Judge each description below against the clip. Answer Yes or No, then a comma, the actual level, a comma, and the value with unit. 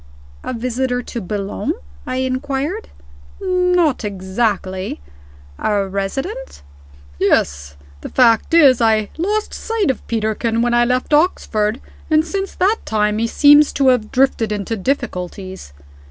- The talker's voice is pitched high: Yes, high, 240 Hz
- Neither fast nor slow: No, slow, 125 wpm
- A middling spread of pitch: No, wide, 5.7 semitones